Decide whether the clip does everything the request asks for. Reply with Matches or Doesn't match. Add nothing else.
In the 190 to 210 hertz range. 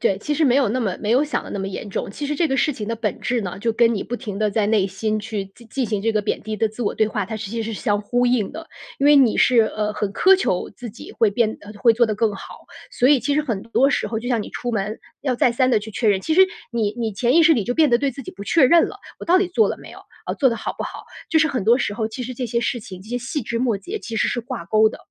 Doesn't match